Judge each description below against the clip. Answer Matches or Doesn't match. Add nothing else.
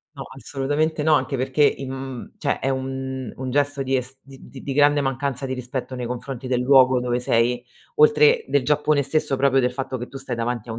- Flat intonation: Matches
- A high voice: Doesn't match